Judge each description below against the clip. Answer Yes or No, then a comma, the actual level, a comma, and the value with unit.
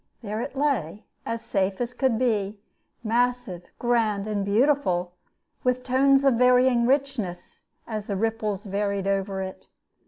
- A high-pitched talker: Yes, high, 225 Hz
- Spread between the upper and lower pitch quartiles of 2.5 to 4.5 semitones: Yes, average, 4.1 semitones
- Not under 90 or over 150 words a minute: Yes, slow, 135 wpm